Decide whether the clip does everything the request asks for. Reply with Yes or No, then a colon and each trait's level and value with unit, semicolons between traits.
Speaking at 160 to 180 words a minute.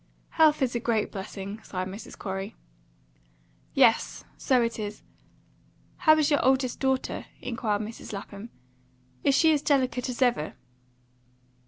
No: slow, 135 wpm